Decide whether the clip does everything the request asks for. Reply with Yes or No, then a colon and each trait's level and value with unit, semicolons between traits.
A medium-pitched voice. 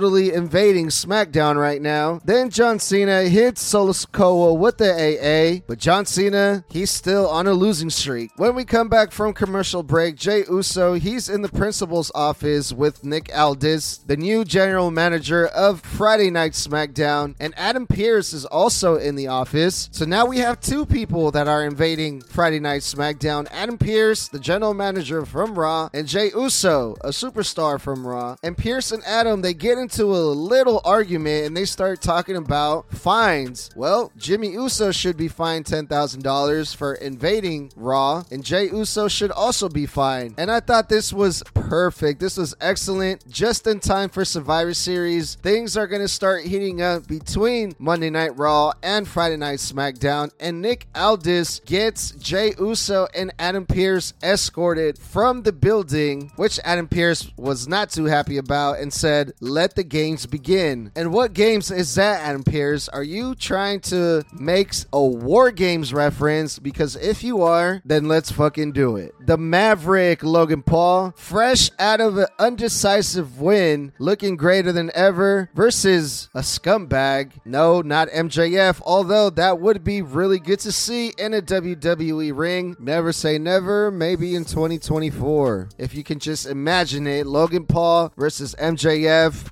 Yes: medium, 170 Hz